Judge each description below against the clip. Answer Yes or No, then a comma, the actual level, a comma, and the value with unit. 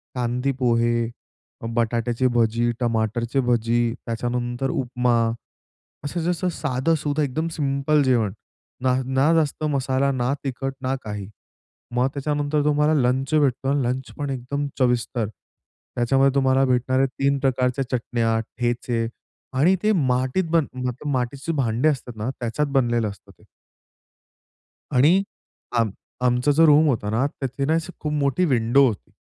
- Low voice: Yes, low, 130 Hz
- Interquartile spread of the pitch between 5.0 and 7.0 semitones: No, average, 2.9 semitones